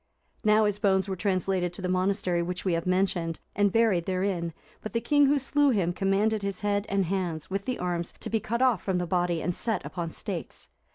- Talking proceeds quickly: Yes, fast, 220 wpm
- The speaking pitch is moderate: No, high, 195 Hz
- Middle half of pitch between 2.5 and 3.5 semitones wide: Yes, average, 3.0 semitones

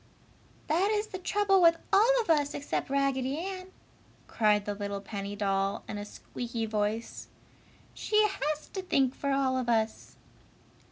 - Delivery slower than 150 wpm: No, average, 155 wpm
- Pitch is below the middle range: No, very high, 270 Hz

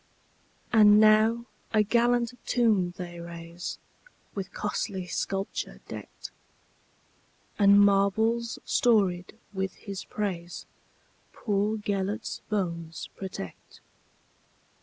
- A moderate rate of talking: No, slow, 75 wpm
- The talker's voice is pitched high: Yes, high, 200 Hz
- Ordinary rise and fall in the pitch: Yes, average, 3.0 semitones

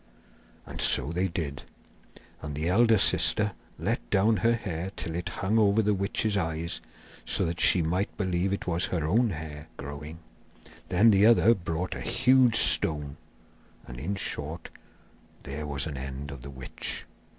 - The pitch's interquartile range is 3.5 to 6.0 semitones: Yes, average, 5.3 semitones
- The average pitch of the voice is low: Yes, very low, 85 Hz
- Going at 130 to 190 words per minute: Yes, average, 160 wpm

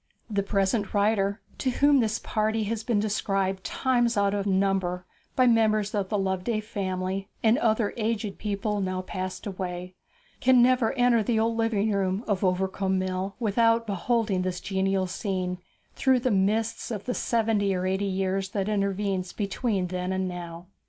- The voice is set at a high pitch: Yes, high, 200 Hz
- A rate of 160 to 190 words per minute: Yes, average, 165 wpm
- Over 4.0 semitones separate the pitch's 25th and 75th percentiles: No, average, 2.8 semitones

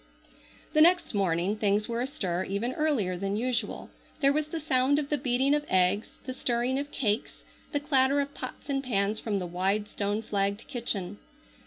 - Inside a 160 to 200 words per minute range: Yes, average, 180 wpm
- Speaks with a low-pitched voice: No, high, 235 Hz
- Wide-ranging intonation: Yes, wide, 5.7 semitones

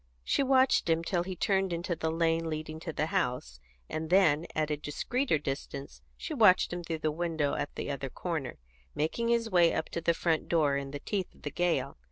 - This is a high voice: No, medium, 165 Hz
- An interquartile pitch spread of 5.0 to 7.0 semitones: No, average, 3.1 semitones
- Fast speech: Yes, fast, 215 wpm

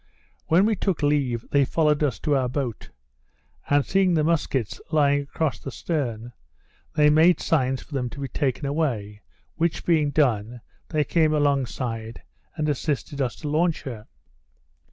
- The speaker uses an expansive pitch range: No, average, 3.6 semitones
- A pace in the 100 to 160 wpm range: Yes, average, 155 wpm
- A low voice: No, medium, 145 Hz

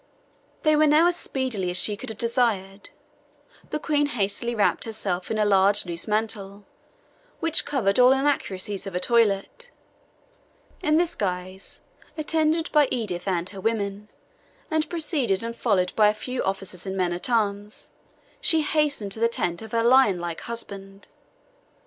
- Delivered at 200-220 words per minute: No, average, 155 wpm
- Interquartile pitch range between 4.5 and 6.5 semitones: Yes, wide, 5.5 semitones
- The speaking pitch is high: Yes, high, 215 Hz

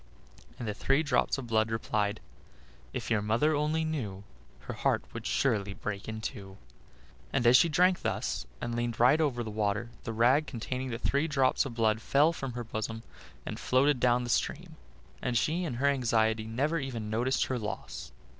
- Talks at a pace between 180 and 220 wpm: Yes, average, 185 wpm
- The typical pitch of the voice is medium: No, low, 120 Hz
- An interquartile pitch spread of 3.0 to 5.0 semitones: Yes, average, 4.0 semitones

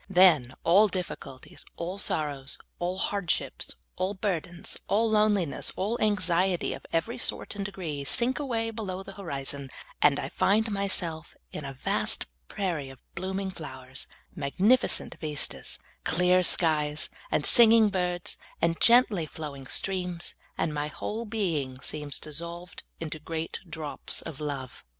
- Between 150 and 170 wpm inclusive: No, average, 140 wpm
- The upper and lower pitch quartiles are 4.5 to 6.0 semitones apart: Yes, average, 4.8 semitones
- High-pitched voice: No, medium, 175 Hz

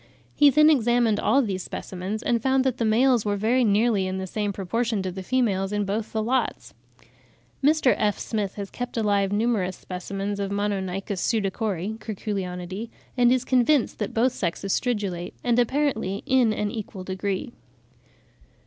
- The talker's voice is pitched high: Yes, high, 210 Hz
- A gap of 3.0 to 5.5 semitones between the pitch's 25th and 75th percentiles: Yes, average, 3.7 semitones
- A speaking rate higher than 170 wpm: No, average, 160 wpm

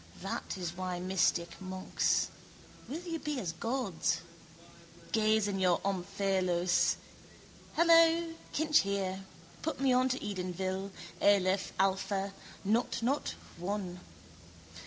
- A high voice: Yes, high, 195 Hz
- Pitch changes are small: No, average, 5.2 semitones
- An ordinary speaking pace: No, slow, 110 wpm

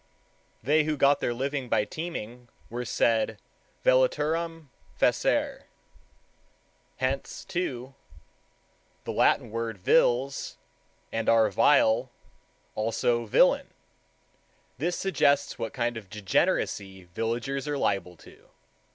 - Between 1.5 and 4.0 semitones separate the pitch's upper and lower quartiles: No, average, 4.6 semitones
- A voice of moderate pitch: No, low, 125 Hz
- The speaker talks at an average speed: No, slow, 100 wpm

